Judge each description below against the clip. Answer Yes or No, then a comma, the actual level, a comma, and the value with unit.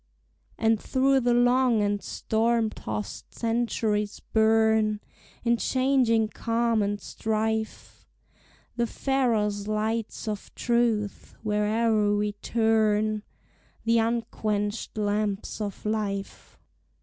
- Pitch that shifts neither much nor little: No, narrow, 1.8 semitones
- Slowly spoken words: Yes, slow, 95 wpm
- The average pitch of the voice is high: Yes, high, 220 Hz